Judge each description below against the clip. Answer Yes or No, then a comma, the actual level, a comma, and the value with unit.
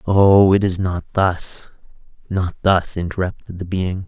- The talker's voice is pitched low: Yes, very low, 95 Hz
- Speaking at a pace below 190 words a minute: Yes, slow, 135 wpm